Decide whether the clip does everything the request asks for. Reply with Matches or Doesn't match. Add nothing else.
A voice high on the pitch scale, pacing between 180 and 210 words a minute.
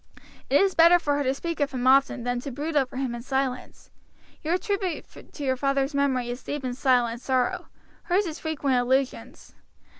Matches